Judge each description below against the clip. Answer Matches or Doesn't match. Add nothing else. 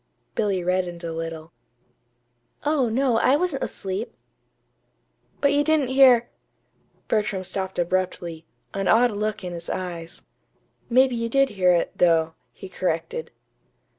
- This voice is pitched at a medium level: Doesn't match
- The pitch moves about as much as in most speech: Doesn't match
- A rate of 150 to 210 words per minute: Doesn't match